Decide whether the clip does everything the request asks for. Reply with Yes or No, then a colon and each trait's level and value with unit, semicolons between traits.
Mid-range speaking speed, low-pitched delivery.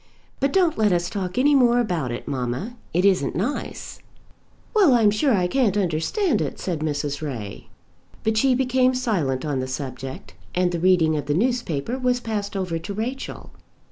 No: average, 175 wpm; high, 190 Hz